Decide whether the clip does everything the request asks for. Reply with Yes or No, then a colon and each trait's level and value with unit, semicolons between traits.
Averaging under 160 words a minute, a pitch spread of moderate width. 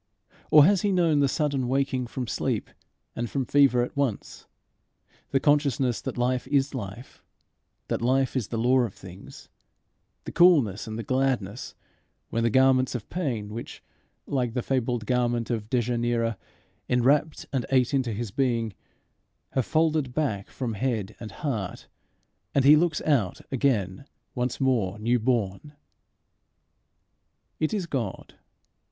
Yes: average, 145 wpm; average, 3.2 semitones